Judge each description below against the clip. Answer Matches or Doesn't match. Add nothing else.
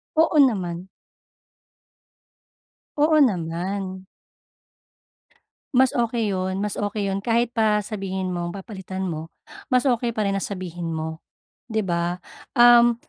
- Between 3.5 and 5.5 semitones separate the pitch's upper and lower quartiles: Matches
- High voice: Matches